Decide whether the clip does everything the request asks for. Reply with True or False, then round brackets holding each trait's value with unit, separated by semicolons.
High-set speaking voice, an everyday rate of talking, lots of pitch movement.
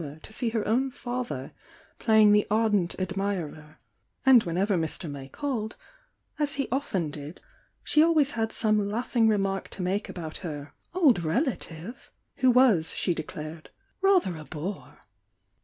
True (205 Hz; 150 wpm; 6.8 semitones)